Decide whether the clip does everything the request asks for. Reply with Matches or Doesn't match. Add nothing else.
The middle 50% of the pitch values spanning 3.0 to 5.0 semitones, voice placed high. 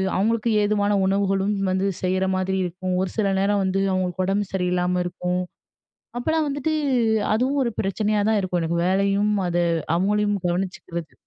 Doesn't match